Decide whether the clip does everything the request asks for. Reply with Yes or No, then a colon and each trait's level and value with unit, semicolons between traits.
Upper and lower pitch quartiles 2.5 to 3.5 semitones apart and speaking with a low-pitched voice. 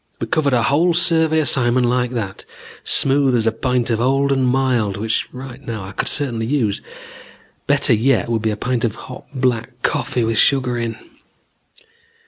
Yes: average, 3.0 semitones; low, 125 Hz